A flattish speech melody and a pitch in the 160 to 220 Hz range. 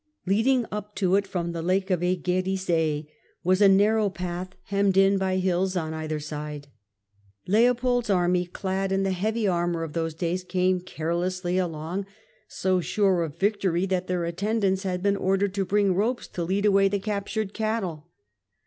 Yes: narrow, 2.3 semitones; medium, 185 Hz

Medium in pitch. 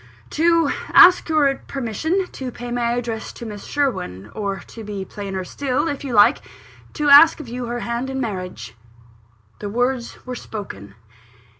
No: high, 240 Hz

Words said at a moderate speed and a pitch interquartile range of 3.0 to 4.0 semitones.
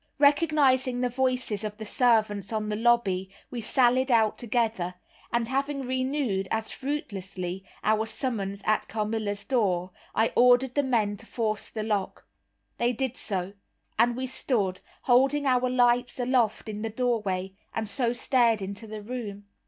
Yes: average, 150 wpm; average, 3.5 semitones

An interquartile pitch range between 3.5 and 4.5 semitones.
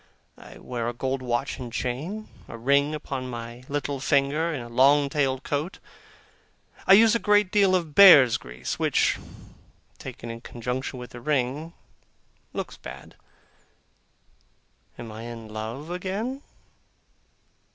No: average, 5.1 semitones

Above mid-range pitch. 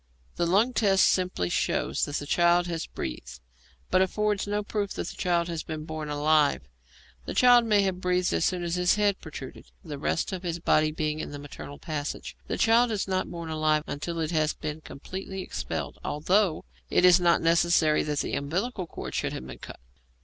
No: medium, 170 Hz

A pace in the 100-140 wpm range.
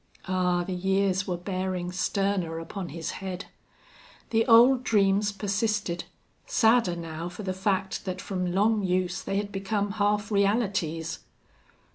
Yes: slow, 135 wpm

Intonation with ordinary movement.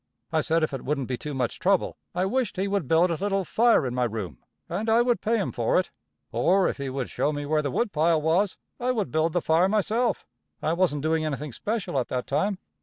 No: wide, 5.7 semitones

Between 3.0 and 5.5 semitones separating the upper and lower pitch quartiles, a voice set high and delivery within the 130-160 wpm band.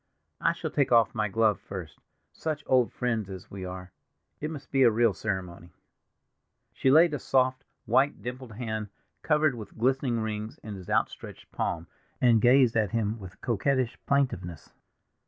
No: average, 4.3 semitones; low, 115 Hz; average, 155 wpm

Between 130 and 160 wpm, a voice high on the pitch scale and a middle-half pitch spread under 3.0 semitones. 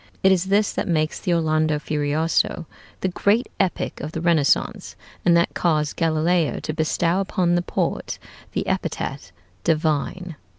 No: average, 145 wpm; medium, 165 Hz; narrow, 2.5 semitones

